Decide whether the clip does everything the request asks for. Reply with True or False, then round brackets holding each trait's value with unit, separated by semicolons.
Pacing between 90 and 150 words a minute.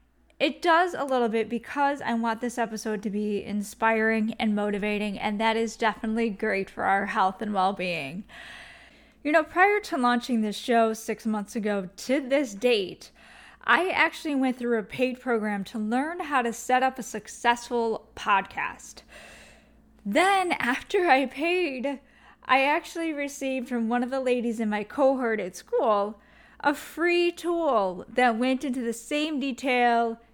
False (160 wpm)